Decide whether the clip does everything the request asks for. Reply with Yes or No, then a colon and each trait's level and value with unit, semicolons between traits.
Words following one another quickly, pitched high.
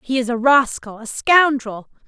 No: average, 175 wpm; very high, 250 Hz